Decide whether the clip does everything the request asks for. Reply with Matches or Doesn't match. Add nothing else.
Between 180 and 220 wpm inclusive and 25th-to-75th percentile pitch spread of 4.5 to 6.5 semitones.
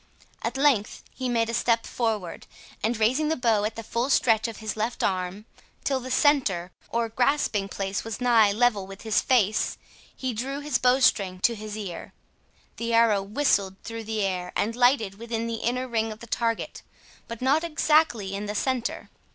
Doesn't match